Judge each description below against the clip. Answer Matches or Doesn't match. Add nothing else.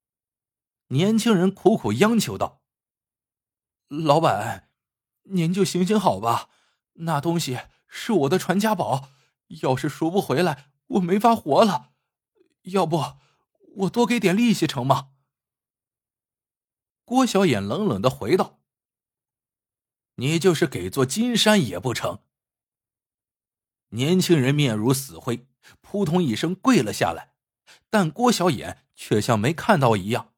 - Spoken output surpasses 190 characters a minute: Doesn't match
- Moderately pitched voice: Matches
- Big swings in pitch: Matches